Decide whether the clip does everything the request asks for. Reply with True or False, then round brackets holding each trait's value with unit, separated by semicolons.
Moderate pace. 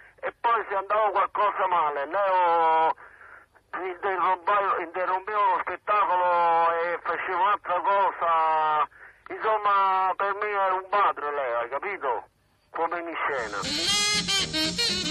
False (105 wpm)